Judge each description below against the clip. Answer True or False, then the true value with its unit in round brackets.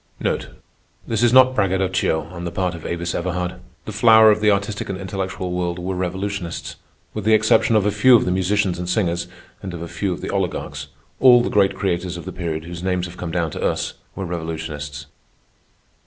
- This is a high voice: False (90 Hz)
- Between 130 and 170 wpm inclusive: False (200 wpm)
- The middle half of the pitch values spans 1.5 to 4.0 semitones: True (2.8 semitones)